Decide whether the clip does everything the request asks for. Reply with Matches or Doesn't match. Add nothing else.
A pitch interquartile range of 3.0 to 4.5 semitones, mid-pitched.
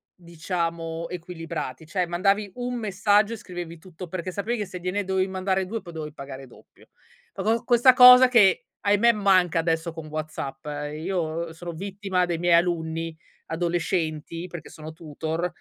Matches